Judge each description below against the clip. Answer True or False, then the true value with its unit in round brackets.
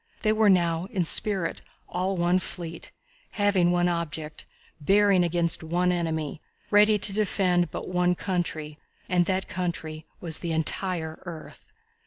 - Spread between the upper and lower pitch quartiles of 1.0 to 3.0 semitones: True (2.4 semitones)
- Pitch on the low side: False (175 Hz)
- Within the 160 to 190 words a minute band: False (140 wpm)